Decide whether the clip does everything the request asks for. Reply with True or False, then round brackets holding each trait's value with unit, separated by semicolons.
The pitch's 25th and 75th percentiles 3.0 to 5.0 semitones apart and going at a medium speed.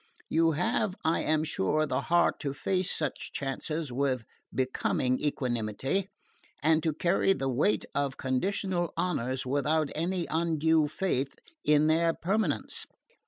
False (4.0 semitones; 130 wpm)